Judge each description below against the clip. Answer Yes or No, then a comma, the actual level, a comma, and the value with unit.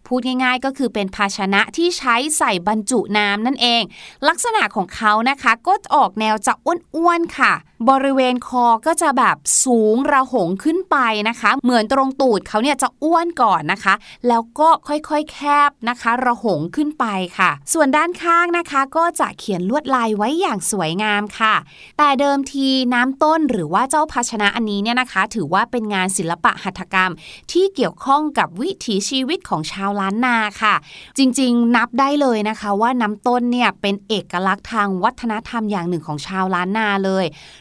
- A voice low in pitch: No, high, 240 Hz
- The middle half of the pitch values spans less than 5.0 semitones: No, wide, 5.4 semitones